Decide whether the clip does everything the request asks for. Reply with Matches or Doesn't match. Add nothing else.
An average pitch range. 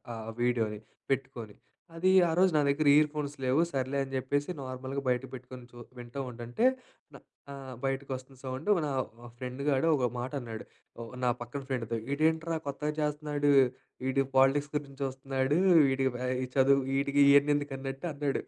Doesn't match